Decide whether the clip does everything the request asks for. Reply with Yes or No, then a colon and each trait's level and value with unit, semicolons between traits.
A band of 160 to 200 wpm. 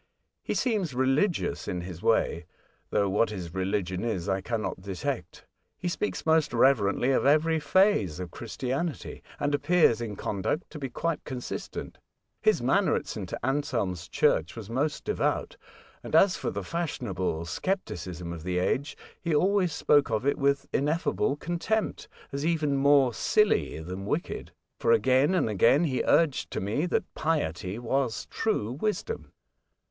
No: average, 150 wpm